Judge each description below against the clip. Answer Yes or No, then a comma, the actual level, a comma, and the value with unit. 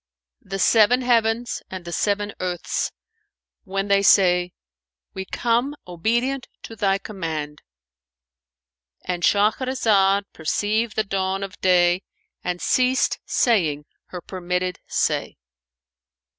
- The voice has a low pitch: No, high, 190 Hz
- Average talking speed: No, slow, 105 wpm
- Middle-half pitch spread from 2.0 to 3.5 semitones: No, average, 3.9 semitones